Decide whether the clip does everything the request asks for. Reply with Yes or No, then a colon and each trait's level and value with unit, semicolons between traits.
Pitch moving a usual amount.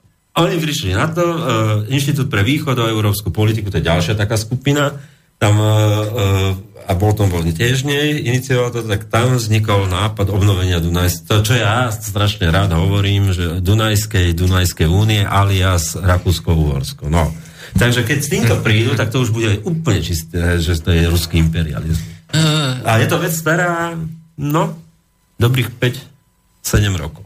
No: wide, 6.0 semitones